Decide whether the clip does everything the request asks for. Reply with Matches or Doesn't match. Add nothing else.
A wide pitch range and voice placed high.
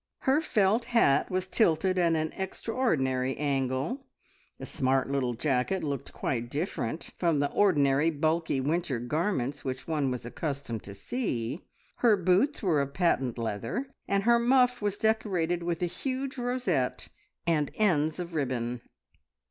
Doesn't match